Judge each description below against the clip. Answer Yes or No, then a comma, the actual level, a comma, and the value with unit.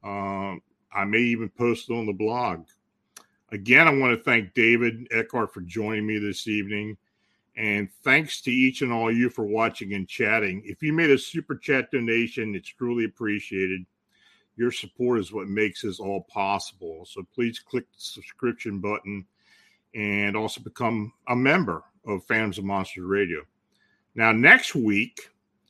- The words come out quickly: No, average, 165 wpm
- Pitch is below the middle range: Yes, low, 110 Hz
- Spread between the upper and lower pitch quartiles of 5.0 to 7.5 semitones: No, average, 3.2 semitones